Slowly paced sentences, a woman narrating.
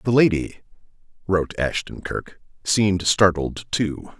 No: slow, 115 wpm; male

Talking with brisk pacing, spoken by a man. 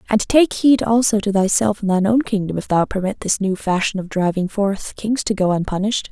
No: fast, 225 wpm; female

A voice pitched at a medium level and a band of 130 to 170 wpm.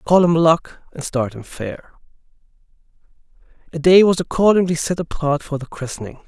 Yes: medium, 155 Hz; average, 155 wpm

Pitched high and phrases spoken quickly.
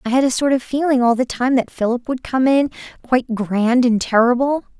Yes: very high, 250 Hz; fast, 225 wpm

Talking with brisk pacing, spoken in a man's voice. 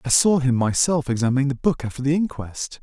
Yes: fast, 210 wpm; male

